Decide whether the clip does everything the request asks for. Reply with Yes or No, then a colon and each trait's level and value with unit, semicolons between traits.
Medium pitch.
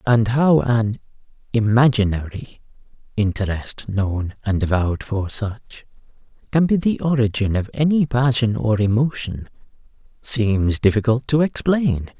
No: low, 115 Hz